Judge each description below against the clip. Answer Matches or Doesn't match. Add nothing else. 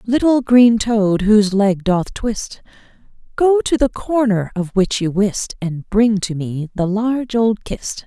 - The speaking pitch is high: Matches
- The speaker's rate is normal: Matches